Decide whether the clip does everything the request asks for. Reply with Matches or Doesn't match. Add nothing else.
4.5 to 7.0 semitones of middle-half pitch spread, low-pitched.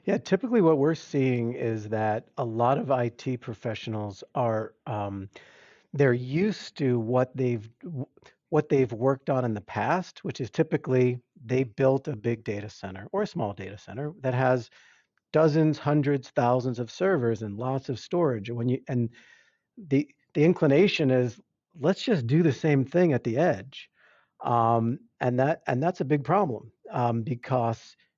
Matches